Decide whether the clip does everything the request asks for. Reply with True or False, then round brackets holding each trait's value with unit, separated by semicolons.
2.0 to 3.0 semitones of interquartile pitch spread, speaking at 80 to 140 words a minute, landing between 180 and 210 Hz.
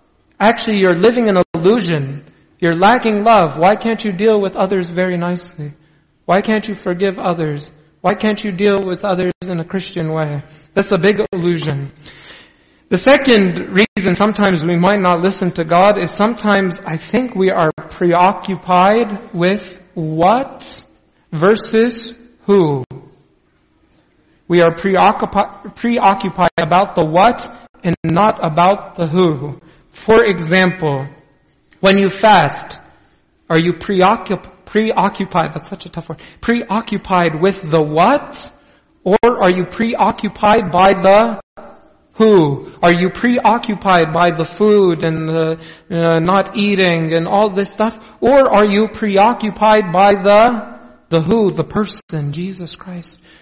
False (3.8 semitones; 135 wpm; 190 Hz)